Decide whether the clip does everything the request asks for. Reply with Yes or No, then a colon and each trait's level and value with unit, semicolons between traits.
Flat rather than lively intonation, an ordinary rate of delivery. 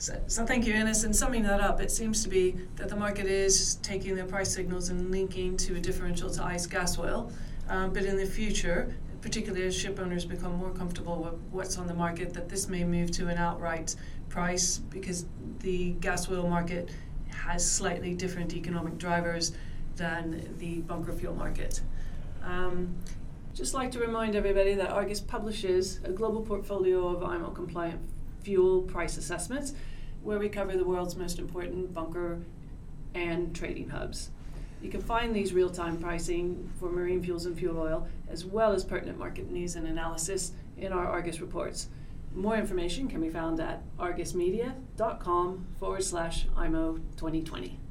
Yes: narrow, 1.9 semitones; average, 170 wpm